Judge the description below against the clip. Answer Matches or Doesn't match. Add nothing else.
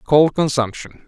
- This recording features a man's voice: Matches